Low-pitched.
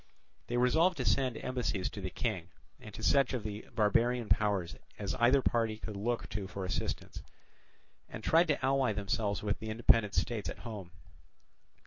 Yes: low, 110 Hz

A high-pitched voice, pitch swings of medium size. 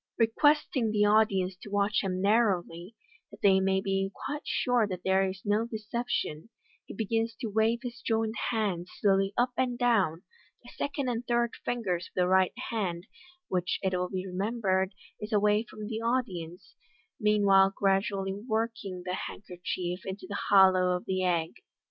Yes: high, 200 Hz; average, 3.3 semitones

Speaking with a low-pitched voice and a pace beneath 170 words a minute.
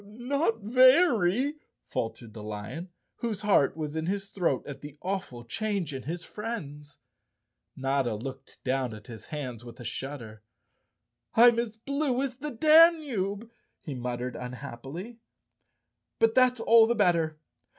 No: medium, 175 Hz; average, 140 wpm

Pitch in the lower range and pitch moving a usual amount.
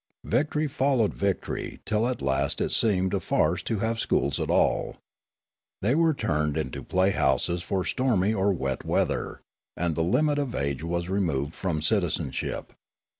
No: very low, 95 Hz; wide, 6.6 semitones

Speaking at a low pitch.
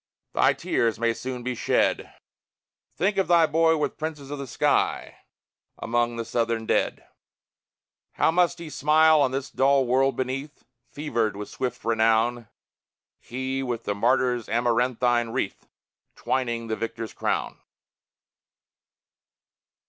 Yes: low, 125 Hz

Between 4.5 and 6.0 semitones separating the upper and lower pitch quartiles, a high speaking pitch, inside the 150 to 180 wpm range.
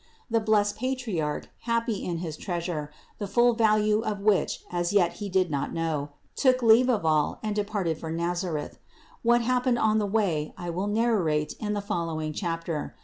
Yes: average, 4.9 semitones; high, 200 Hz; average, 175 wpm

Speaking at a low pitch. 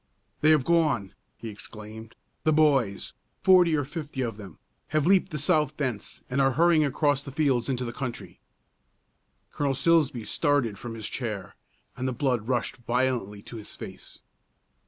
Yes: low, 130 Hz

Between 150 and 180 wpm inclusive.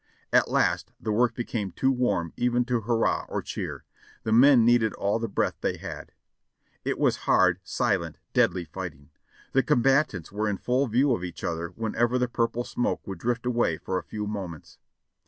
No: average, 190 wpm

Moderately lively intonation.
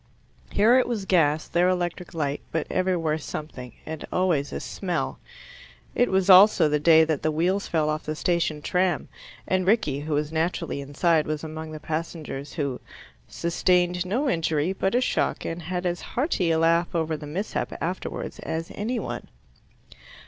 Yes: average, 3.1 semitones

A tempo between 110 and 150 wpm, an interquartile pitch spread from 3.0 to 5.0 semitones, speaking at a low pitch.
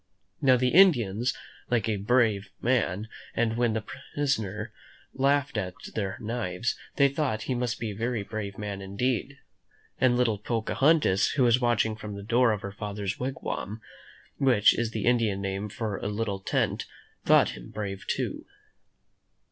No: average, 160 wpm; average, 3.5 semitones; low, 110 Hz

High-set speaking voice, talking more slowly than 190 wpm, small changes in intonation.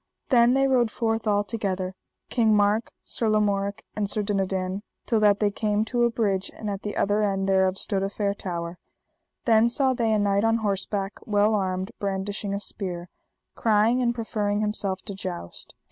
Yes: high, 205 Hz; average, 175 wpm; narrow, 2.2 semitones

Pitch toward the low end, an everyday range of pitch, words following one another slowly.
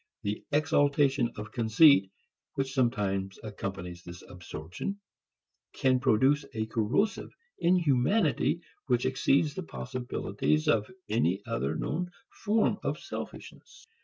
No: low, 125 Hz; wide, 6.0 semitones; slow, 105 wpm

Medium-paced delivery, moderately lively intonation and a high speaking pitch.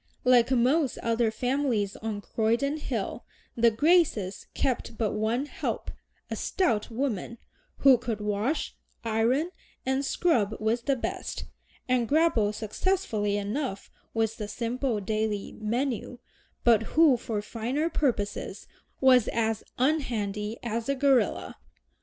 No: slow, 125 wpm; average, 3.8 semitones; high, 235 Hz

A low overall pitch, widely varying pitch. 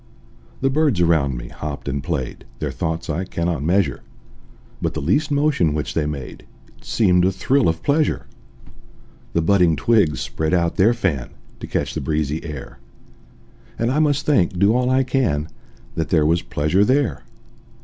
Yes: very low, 85 Hz; wide, 7.7 semitones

